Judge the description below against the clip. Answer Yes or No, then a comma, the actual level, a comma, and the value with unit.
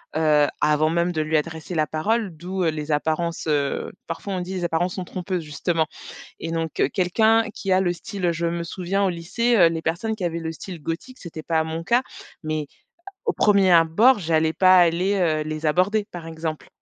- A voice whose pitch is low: No, medium, 170 Hz